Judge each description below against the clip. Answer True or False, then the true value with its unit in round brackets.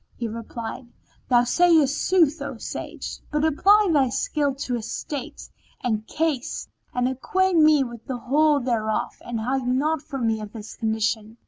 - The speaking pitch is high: True (260 Hz)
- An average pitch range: True (4.7 semitones)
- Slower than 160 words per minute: False (165 wpm)